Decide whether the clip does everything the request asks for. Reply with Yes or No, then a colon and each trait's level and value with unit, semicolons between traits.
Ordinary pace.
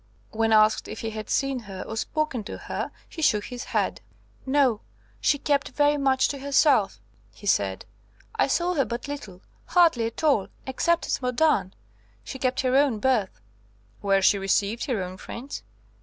Yes: average, 170 wpm